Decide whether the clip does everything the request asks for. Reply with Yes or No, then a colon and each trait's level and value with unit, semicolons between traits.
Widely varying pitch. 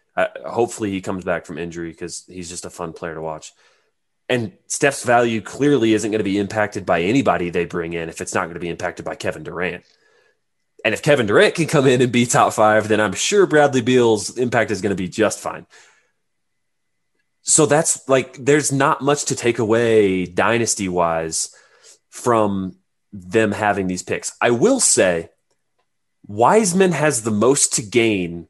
Yes: wide, 5.7 semitones